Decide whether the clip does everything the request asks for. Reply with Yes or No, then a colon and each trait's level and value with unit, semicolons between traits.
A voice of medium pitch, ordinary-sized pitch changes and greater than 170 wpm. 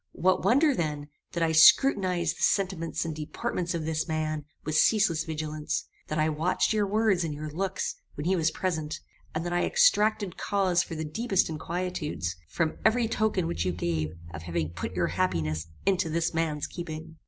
Yes: medium, 165 Hz; average, 3.5 semitones; average, 180 wpm